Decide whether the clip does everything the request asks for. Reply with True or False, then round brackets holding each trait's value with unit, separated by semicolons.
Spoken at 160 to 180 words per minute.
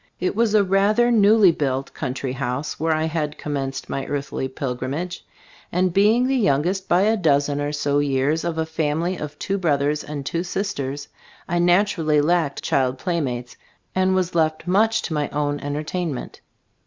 True (165 wpm)